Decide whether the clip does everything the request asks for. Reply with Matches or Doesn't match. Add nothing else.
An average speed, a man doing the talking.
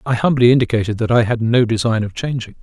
Doesn't match